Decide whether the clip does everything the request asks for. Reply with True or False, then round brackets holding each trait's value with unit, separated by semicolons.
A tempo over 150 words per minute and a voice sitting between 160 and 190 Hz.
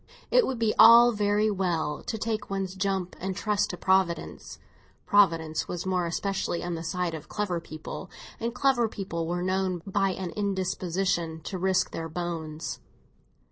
True (160 wpm; 185 Hz)